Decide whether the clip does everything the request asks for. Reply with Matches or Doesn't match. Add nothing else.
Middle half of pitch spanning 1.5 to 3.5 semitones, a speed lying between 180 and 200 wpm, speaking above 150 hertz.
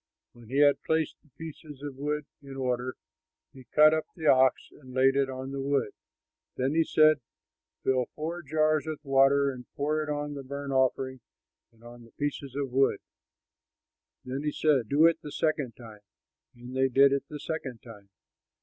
Doesn't match